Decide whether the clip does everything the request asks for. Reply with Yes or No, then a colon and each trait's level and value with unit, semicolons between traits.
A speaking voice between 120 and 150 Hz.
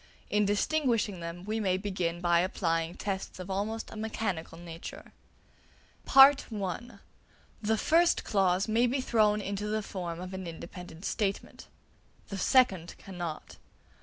No: high, 195 Hz